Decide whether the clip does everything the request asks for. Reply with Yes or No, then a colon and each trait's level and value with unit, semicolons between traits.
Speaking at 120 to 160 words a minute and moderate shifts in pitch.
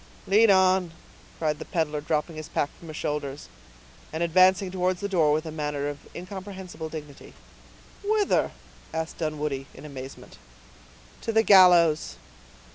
Yes: average, 140 wpm; average, 3.8 semitones